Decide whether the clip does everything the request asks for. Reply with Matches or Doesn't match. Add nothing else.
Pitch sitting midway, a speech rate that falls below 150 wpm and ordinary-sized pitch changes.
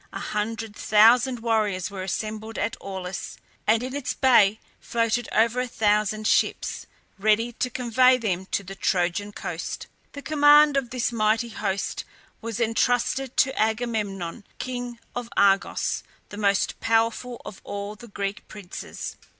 Doesn't match